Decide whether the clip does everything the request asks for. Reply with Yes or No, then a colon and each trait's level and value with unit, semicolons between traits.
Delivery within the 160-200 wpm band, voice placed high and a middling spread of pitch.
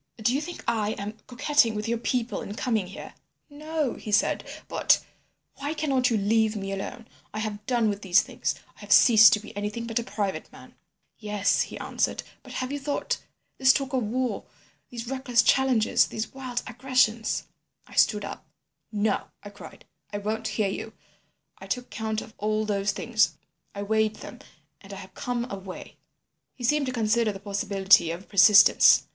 Yes: average, 175 wpm; high, 220 Hz; average, 3.2 semitones